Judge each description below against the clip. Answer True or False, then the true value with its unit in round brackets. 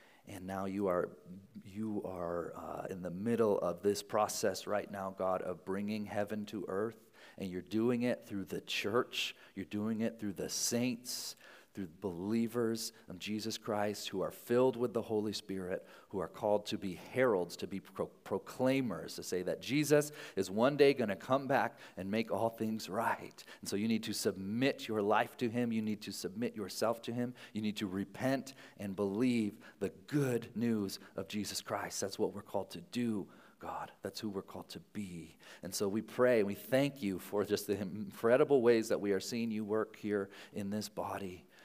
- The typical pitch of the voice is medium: False (105 Hz)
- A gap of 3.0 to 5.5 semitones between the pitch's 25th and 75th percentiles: True (3.3 semitones)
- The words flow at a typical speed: True (195 wpm)